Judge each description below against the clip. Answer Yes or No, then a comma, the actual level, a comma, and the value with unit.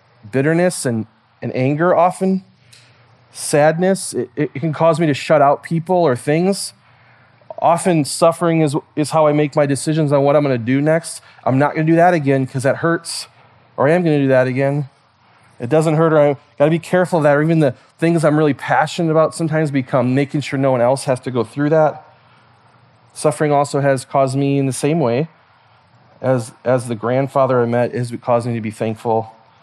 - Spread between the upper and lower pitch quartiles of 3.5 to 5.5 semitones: Yes, average, 3.9 semitones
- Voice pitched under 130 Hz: No, medium, 140 Hz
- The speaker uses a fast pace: Yes, fast, 210 wpm